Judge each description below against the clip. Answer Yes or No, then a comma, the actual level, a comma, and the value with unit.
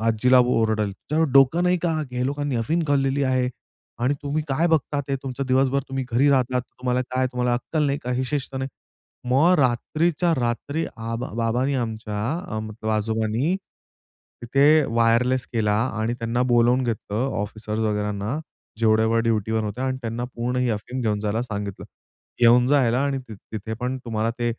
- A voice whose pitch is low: Yes, low, 125 Hz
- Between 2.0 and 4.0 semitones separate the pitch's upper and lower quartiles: Yes, average, 3.3 semitones